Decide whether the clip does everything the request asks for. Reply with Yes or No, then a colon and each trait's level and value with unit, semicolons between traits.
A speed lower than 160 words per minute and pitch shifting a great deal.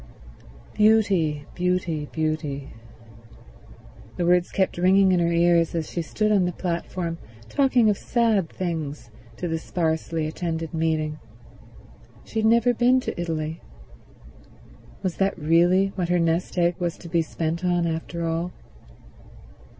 No: slow, 135 wpm; narrow, 2.4 semitones